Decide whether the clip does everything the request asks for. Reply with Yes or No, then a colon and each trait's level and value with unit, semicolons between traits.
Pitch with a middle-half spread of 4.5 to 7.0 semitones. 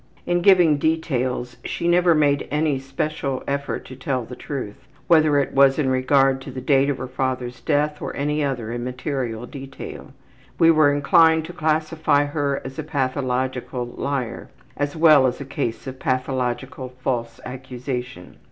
No: average, 2.8 semitones